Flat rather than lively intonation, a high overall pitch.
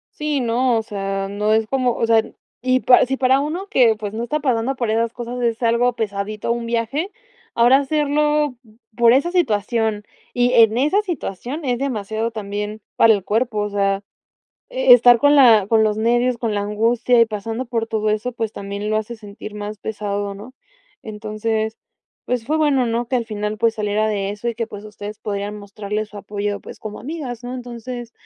No: average, 3.0 semitones; high, 230 Hz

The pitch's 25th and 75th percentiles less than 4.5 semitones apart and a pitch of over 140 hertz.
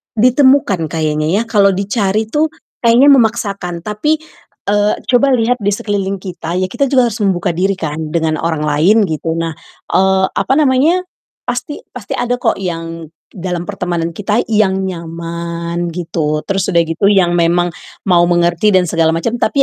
No: average, 4.8 semitones; high, 190 Hz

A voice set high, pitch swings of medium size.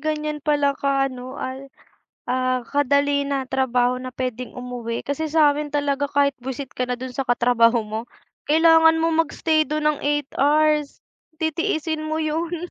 Yes: very high, 285 Hz; average, 3.1 semitones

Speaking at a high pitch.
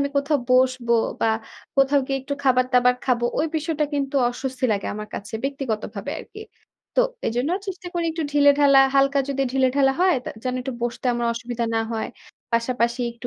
Yes: very high, 265 Hz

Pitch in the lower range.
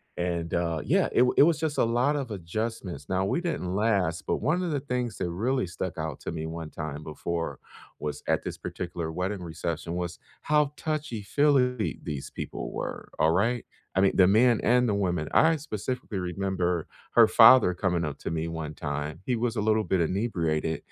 Yes: very low, 95 Hz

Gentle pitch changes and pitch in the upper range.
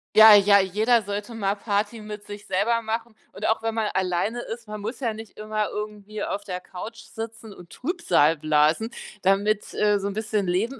Yes: narrow, 2.0 semitones; high, 210 Hz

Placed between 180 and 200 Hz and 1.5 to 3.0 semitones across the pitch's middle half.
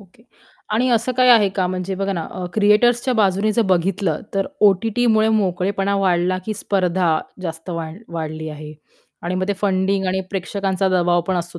Yes: high, 190 Hz; average, 2.7 semitones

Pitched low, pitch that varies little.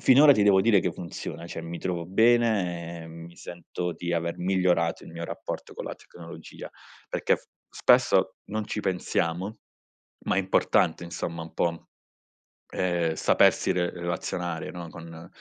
Yes: very low, 85 Hz; narrow, 2.1 semitones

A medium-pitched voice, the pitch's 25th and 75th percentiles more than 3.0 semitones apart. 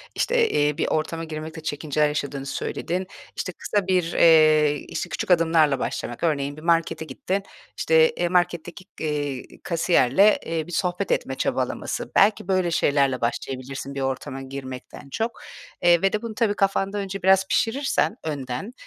Yes: medium, 165 Hz; average, 4.9 semitones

